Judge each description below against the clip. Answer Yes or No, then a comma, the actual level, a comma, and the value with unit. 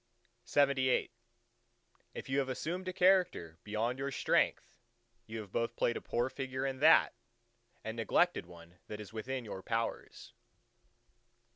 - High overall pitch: No, low, 125 Hz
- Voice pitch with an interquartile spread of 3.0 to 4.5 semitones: Yes, average, 4.2 semitones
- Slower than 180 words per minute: Yes, average, 140 wpm